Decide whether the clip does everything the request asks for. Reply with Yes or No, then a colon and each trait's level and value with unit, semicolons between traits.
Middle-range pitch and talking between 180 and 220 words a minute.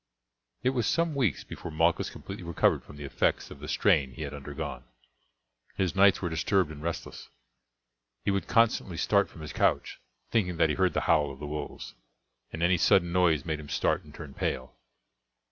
No: very low, 85 Hz; average, 190 wpm